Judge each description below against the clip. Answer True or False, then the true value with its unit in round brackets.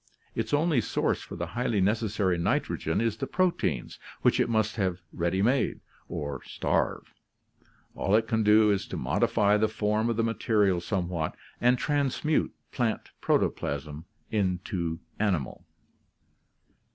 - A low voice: True (105 Hz)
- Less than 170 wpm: True (135 wpm)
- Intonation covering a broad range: False (4.4 semitones)